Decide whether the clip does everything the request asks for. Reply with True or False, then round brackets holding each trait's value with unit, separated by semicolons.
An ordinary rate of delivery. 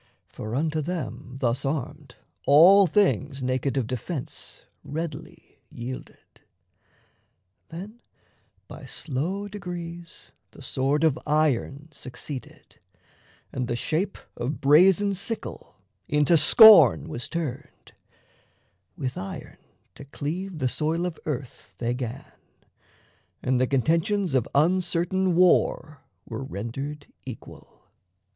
False (105 wpm)